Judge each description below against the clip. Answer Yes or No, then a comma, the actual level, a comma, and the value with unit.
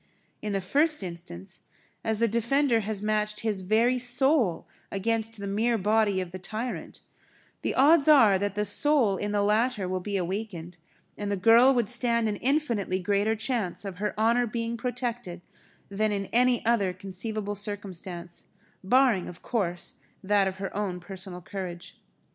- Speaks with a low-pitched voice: No, high, 210 Hz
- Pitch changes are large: No, average, 3.5 semitones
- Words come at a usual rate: Yes, average, 160 wpm